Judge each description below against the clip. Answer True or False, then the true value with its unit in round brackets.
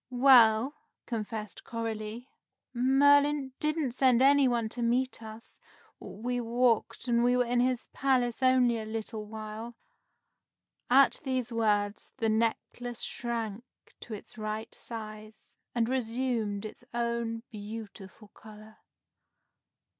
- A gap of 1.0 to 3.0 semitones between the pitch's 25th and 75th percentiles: True (2.5 semitones)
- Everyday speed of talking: False (115 wpm)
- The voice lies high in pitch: True (235 Hz)